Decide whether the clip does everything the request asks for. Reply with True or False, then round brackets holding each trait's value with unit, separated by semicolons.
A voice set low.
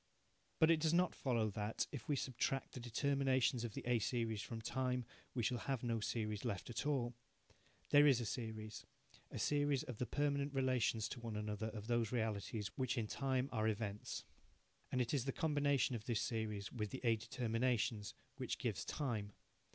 True (120 Hz)